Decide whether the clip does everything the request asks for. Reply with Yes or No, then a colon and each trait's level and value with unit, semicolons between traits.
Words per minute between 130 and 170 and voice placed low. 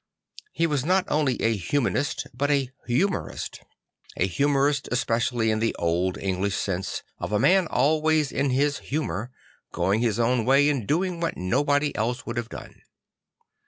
Yes: average, 165 wpm; low, 130 Hz